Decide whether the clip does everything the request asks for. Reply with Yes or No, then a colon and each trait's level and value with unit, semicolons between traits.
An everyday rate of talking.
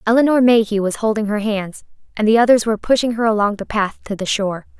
No: fast, 225 wpm